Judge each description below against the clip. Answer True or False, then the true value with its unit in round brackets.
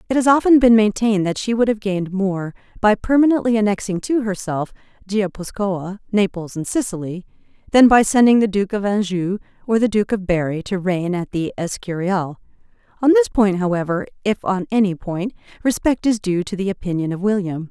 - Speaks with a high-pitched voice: True (200 Hz)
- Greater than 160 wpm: True (180 wpm)